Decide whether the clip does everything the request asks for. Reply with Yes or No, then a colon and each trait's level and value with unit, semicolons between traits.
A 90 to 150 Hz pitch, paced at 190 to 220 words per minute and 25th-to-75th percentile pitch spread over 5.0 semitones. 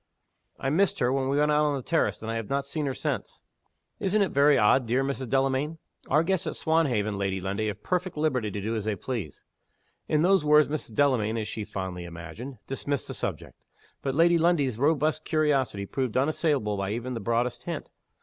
Yes: low, 135 Hz; fast, 205 wpm; wide, 5.6 semitones